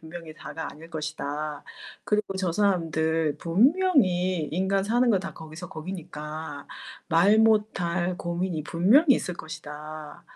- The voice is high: No, medium, 170 Hz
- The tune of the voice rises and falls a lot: No, average, 3.7 semitones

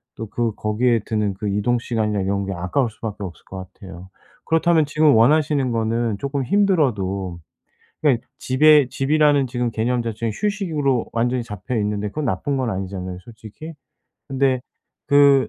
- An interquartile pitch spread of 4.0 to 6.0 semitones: Yes, average, 5.2 semitones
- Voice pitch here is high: No, low, 120 Hz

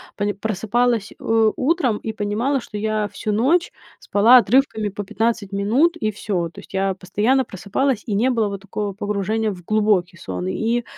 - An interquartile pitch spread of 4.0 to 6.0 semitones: No, average, 2.8 semitones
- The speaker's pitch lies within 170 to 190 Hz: No, high, 215 Hz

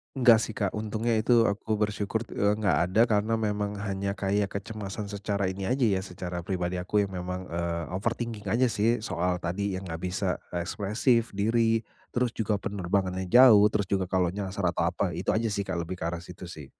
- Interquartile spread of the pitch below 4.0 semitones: Yes, average, 2.9 semitones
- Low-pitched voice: Yes, low, 100 Hz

